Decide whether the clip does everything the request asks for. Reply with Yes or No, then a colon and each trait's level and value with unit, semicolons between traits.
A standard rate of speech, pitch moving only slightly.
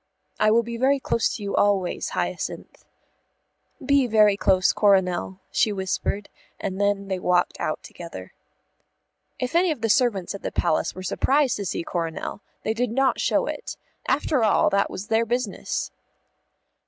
No: average, 160 wpm; average, 4.1 semitones